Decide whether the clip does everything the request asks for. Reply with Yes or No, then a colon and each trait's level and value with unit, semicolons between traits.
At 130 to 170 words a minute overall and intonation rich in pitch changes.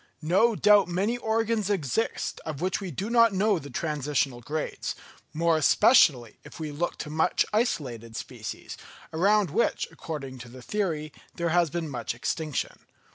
Yes: average, 155 wpm; wide, 6.2 semitones